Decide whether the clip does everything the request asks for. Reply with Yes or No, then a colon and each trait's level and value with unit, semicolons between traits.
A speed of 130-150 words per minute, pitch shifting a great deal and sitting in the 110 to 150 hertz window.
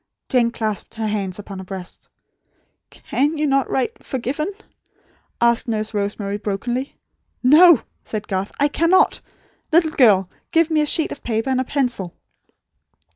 No: average, 145 wpm; wide, 5.9 semitones; high, 240 Hz